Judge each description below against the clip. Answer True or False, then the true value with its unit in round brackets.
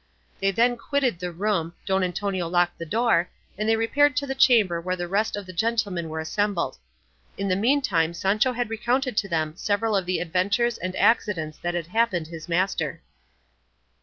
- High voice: True (195 Hz)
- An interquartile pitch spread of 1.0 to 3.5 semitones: False (4.6 semitones)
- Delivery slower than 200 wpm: True (185 wpm)